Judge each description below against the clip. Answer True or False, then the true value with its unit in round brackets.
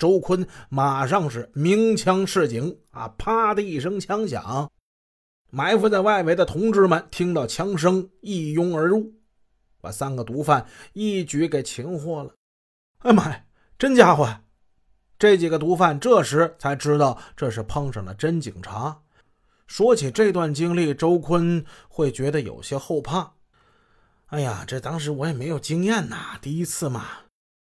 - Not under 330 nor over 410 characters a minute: False (215 characters per minute)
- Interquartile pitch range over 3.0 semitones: True (5.2 semitones)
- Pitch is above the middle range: False (160 Hz)